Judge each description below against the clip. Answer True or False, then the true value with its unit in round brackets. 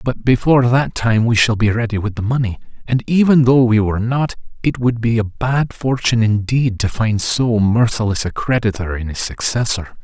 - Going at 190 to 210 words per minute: True (195 wpm)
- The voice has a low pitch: True (115 Hz)